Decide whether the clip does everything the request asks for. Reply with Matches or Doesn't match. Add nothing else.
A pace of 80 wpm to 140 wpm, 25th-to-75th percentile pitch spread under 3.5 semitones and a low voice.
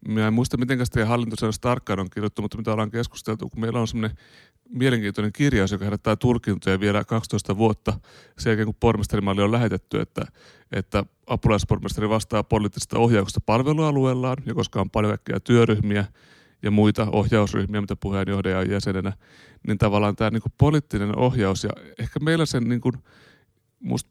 Doesn't match